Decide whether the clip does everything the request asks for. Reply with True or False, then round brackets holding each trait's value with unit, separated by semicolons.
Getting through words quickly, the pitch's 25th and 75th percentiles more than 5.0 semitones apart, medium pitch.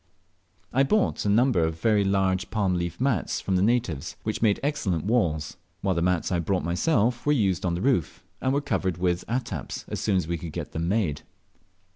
False (215 wpm; 5.4 semitones; 95 Hz)